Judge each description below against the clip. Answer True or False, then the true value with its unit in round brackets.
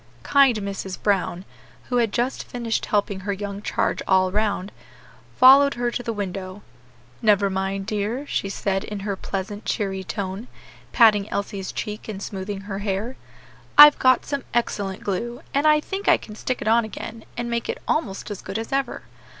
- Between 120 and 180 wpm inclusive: True (175 wpm)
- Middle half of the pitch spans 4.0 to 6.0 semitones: False (3.5 semitones)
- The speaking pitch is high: True (210 Hz)